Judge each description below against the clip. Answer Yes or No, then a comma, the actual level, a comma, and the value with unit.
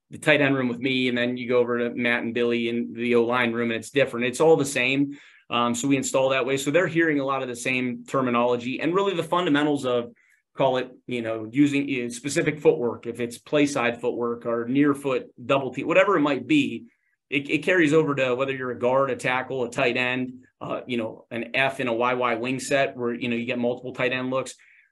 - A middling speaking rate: No, fast, 240 wpm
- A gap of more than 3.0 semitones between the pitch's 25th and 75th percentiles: No, average, 2.7 semitones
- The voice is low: Yes, low, 125 Hz